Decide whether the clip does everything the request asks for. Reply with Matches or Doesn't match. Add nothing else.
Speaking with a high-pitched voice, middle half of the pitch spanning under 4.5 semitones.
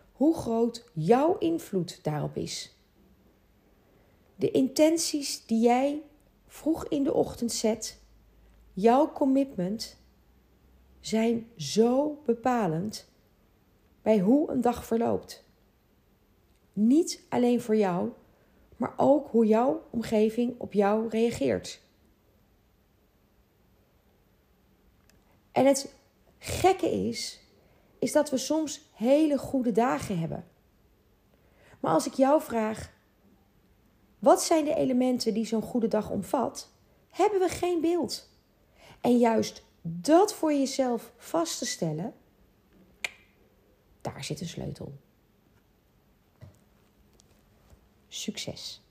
Doesn't match